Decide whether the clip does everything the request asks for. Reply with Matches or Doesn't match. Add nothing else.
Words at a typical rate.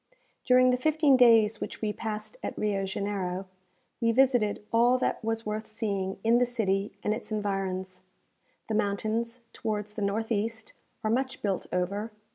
Matches